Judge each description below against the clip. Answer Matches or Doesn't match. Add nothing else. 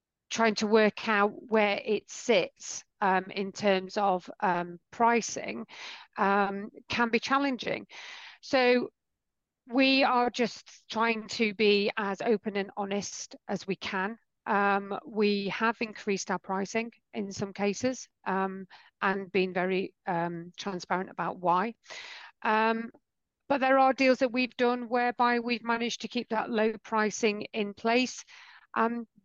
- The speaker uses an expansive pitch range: Doesn't match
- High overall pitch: Matches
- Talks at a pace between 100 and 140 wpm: Matches